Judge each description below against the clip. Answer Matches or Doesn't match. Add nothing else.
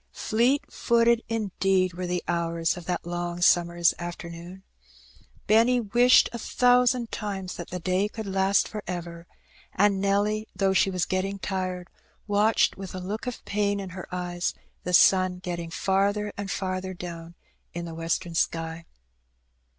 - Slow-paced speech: Doesn't match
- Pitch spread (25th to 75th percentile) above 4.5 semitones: Doesn't match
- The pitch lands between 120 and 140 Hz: Doesn't match